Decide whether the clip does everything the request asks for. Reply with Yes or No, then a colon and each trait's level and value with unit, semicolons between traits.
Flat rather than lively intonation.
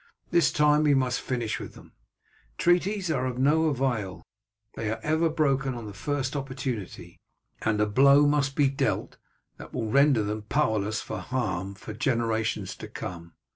No: average, 5.0 semitones